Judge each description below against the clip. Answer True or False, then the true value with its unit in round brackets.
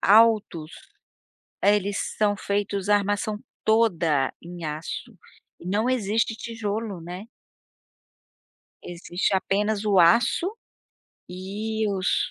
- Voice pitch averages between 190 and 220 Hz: True (205 Hz)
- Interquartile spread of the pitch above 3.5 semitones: False (3.0 semitones)